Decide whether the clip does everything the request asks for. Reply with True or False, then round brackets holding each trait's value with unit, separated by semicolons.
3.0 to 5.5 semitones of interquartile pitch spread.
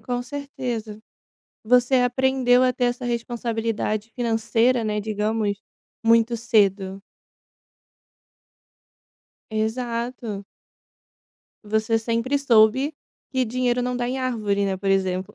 False (2.5 semitones)